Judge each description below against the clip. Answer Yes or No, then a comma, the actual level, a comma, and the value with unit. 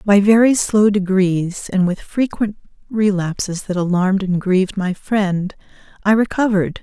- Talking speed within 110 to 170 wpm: Yes, average, 140 wpm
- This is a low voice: No, high, 195 Hz